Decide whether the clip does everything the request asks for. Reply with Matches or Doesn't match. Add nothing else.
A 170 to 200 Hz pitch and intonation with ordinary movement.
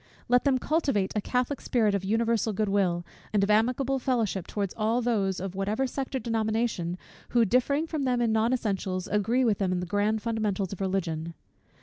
Doesn't match